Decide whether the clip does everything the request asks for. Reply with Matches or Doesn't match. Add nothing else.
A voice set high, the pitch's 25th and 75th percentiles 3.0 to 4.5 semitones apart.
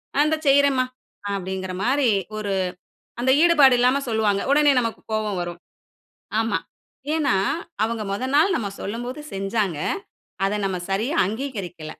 Doesn't match